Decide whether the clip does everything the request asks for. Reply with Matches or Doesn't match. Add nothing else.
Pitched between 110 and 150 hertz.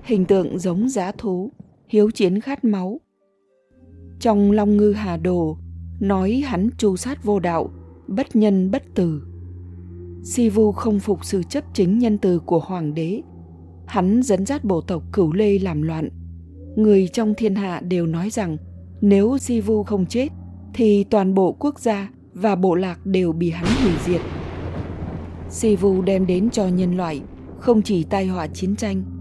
Doesn't match